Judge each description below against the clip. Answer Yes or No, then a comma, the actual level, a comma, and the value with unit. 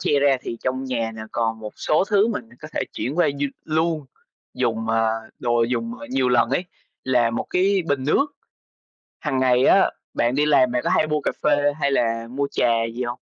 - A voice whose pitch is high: No, low, 130 Hz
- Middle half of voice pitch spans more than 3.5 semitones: Yes, average, 4.2 semitones